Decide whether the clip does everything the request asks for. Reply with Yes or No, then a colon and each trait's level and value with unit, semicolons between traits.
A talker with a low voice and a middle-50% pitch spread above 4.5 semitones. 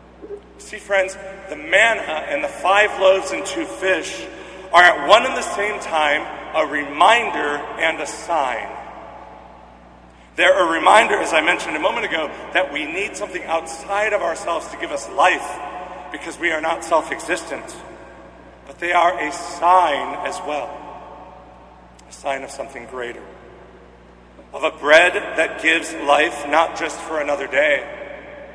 No: medium, 175 Hz; average, 5.0 semitones